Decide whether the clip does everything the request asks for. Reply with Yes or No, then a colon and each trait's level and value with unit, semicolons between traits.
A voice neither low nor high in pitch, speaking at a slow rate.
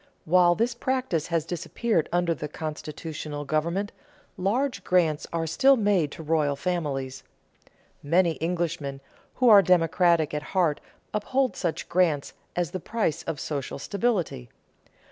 Yes: medium, 170 Hz; slow, 125 wpm